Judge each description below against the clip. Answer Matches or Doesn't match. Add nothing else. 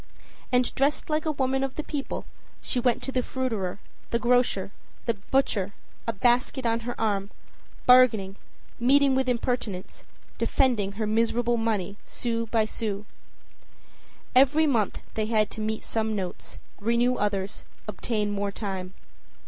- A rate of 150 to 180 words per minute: Doesn't match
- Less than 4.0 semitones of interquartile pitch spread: Matches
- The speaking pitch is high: Matches